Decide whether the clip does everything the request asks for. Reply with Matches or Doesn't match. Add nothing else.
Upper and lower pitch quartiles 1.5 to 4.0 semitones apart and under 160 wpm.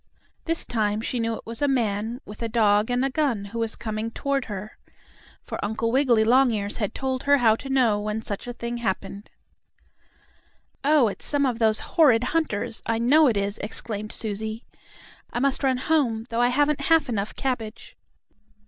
Doesn't match